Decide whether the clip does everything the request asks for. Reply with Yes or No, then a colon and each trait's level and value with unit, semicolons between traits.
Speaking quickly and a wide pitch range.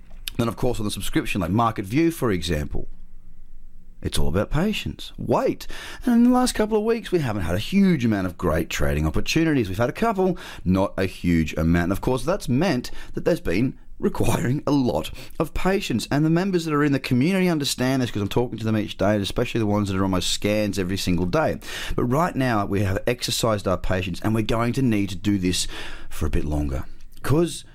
Yes: fast, 225 wpm; wide, 6.8 semitones